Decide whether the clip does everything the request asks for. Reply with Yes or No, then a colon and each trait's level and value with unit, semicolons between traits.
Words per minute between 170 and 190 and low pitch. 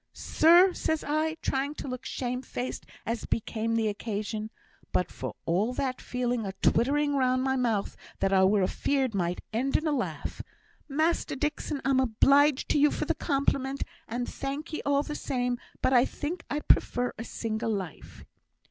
No: average, 175 wpm; very high, 255 Hz